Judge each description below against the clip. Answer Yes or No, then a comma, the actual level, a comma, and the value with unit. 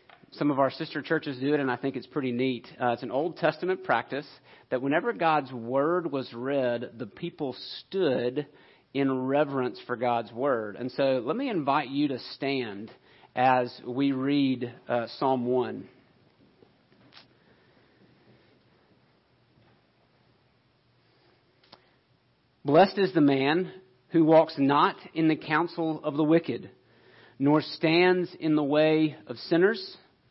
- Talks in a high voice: No, medium, 140 Hz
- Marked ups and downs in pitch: No, average, 4.0 semitones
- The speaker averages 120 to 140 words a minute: Yes, slow, 135 wpm